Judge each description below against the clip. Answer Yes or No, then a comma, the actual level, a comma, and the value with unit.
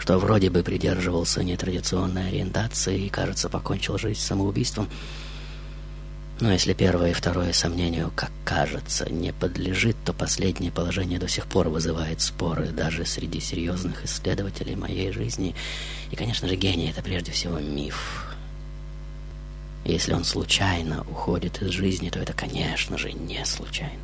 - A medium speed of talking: Yes, average, 140 wpm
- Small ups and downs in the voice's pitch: Yes, narrow, 1.9 semitones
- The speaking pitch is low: Yes, very low, 90 Hz